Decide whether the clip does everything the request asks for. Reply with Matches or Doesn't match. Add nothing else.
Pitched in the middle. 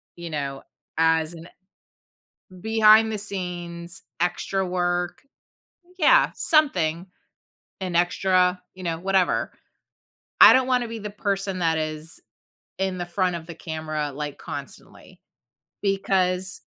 Matches